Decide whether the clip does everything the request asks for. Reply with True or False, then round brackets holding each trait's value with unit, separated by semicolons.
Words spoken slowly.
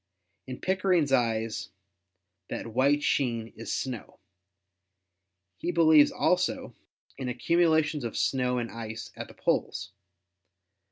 True (115 wpm)